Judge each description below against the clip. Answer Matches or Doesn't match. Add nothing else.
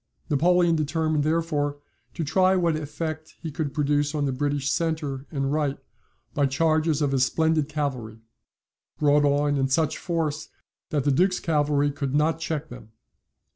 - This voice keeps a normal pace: Matches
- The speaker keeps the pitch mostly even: Matches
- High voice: Doesn't match